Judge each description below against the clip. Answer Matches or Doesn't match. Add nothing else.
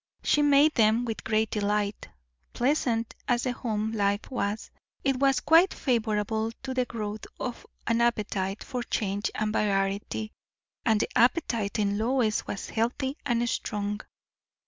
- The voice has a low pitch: Doesn't match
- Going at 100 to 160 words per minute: Matches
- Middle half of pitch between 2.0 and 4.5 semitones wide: Matches